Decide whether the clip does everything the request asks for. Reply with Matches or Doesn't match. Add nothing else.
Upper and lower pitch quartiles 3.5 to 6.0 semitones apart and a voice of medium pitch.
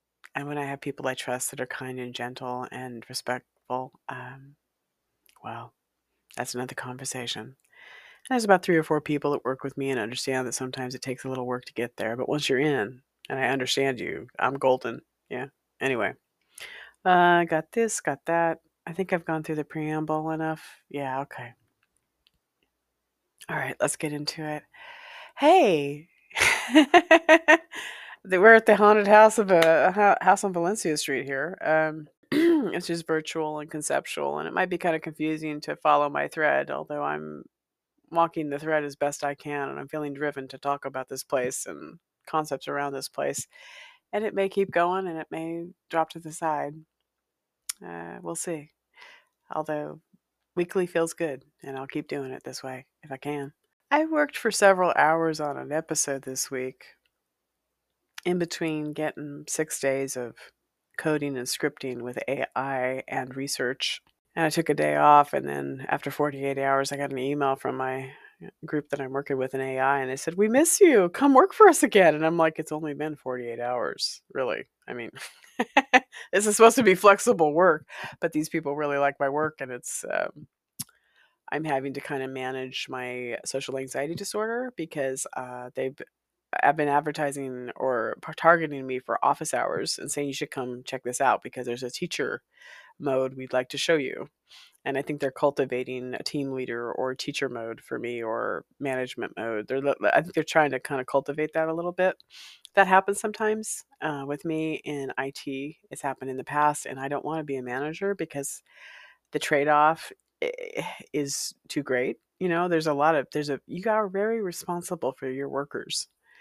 Matches